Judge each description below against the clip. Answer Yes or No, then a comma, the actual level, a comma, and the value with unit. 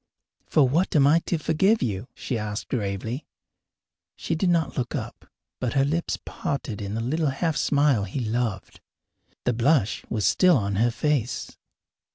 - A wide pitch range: Yes, wide, 5.7 semitones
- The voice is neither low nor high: No, low, 130 Hz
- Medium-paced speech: Yes, average, 165 wpm